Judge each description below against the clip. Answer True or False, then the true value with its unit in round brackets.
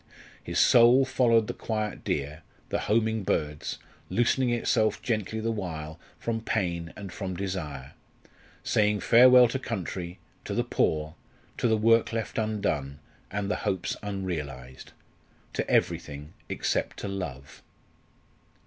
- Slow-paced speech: True (130 wpm)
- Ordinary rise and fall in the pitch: False (6.1 semitones)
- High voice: False (100 Hz)